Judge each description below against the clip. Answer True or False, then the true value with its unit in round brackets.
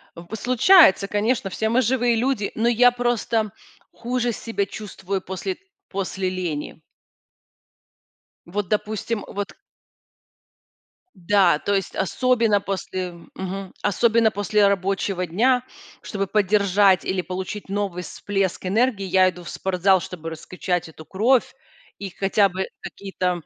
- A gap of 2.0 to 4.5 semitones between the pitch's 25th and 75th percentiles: True (3.1 semitones)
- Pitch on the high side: True (200 Hz)